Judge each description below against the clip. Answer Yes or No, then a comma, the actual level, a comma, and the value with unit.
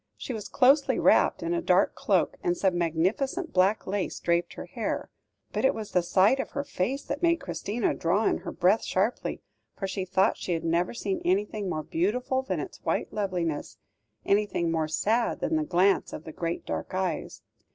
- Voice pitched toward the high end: Yes, high, 195 Hz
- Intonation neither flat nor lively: No, wide, 6.2 semitones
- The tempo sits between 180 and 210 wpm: Yes, average, 195 wpm